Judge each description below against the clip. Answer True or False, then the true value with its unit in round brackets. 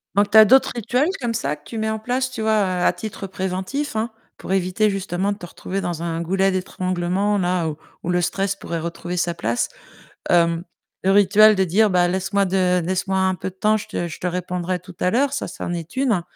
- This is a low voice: False (190 Hz)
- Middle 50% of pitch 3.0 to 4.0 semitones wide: True (3.3 semitones)